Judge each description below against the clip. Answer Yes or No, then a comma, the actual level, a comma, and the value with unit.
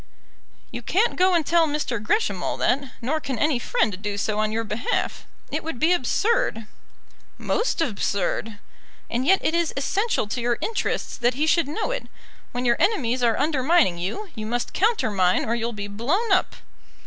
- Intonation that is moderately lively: No, wide, 7.3 semitones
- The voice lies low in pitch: No, very high, 255 Hz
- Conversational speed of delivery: Yes, average, 180 wpm